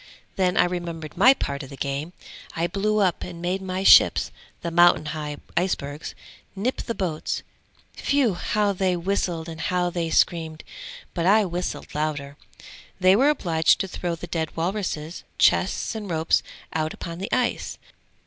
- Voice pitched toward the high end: No, medium, 175 Hz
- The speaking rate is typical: Yes, average, 160 wpm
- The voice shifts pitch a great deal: No, average, 3.1 semitones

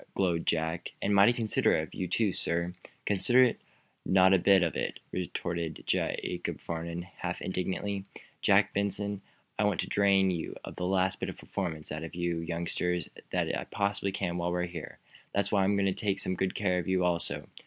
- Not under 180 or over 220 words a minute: Yes, average, 185 wpm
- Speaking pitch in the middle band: No, very low, 95 Hz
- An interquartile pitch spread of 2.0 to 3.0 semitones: Yes, narrow, 2.4 semitones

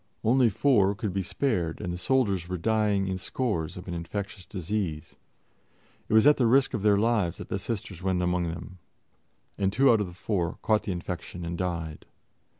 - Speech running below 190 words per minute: No, average, 195 wpm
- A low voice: Yes, very low, 95 Hz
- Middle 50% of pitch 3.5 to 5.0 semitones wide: Yes, average, 3.8 semitones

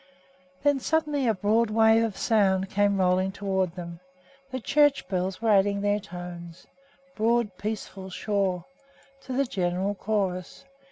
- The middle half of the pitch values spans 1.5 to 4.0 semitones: Yes, average, 3.3 semitones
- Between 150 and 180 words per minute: No, slow, 135 wpm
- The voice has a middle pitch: No, high, 200 Hz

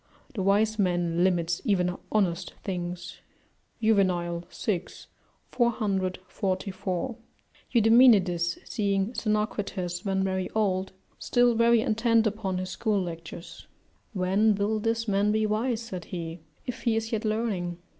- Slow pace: Yes, slow, 120 wpm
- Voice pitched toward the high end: Yes, high, 200 Hz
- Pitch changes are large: No, average, 3.4 semitones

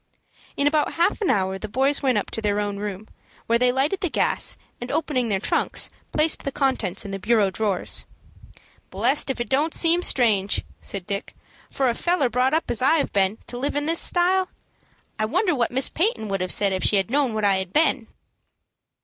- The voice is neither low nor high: No, high, 245 Hz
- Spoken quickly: Yes, fast, 210 wpm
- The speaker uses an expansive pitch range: Yes, wide, 6.3 semitones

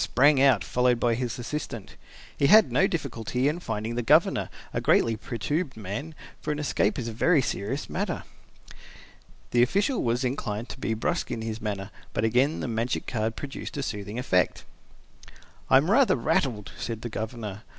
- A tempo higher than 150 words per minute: Yes, average, 175 wpm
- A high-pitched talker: No, low, 120 Hz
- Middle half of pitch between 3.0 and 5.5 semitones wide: Yes, average, 4.2 semitones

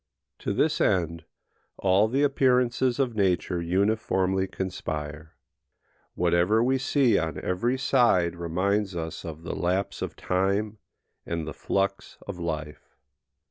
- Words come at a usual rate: No, slow, 125 wpm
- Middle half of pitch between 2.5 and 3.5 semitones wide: No, average, 4.4 semitones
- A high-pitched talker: No, very low, 95 Hz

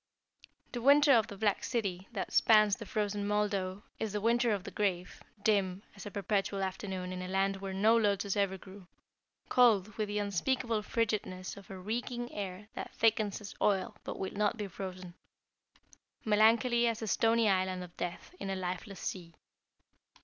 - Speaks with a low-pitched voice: No, high, 205 Hz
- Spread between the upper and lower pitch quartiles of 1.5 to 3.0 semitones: Yes, narrow, 2.6 semitones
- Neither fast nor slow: Yes, average, 175 wpm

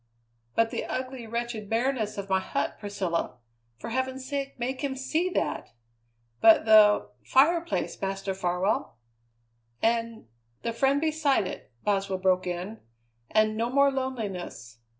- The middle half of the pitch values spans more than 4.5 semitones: Yes, average, 5.2 semitones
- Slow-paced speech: Yes, slow, 130 wpm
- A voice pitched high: Yes, high, 225 Hz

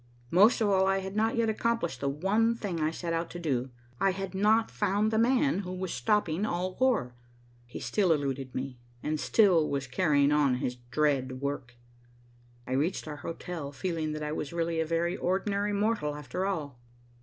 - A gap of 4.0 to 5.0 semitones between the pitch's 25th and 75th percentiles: No, wide, 5.6 semitones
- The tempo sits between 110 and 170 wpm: No, average, 190 wpm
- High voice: No, medium, 170 Hz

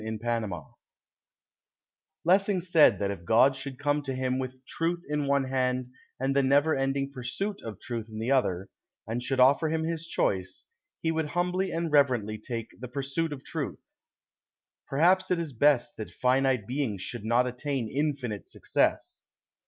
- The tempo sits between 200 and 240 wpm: No, average, 165 wpm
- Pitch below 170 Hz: Yes, low, 135 Hz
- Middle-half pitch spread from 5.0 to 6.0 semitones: No, average, 3.9 semitones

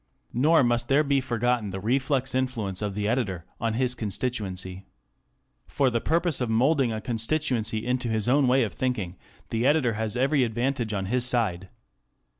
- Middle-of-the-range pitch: No, low, 120 Hz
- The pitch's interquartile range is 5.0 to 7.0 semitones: No, average, 3.4 semitones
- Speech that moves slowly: No, average, 170 wpm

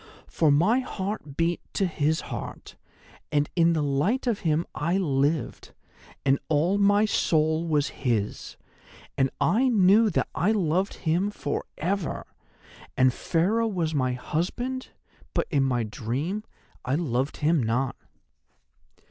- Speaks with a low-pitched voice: No, medium, 160 Hz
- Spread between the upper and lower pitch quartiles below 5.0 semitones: No, wide, 5.6 semitones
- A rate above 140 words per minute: No, slow, 135 wpm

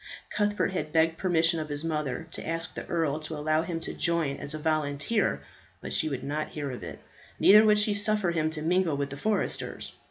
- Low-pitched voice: No, medium, 160 Hz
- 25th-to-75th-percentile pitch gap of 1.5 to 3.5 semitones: Yes, average, 2.9 semitones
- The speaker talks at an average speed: No, fast, 215 wpm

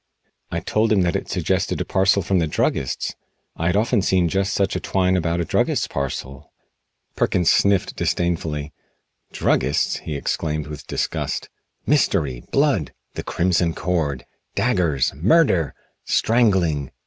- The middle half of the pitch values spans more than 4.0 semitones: Yes, average, 4.5 semitones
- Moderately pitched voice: No, very low, 85 Hz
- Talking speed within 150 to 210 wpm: No, slow, 135 wpm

